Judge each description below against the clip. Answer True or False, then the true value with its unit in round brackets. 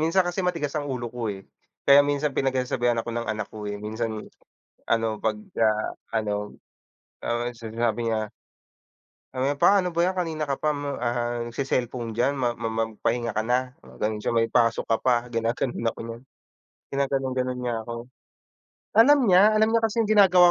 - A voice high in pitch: False (125 Hz)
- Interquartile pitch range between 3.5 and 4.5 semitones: True (4.1 semitones)